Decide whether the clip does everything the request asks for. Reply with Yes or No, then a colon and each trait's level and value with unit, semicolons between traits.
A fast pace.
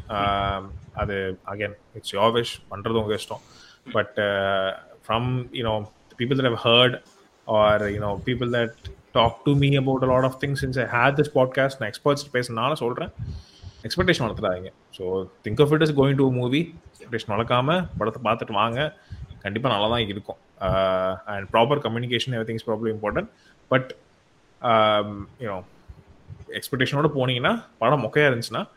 Yes: fast, 140 wpm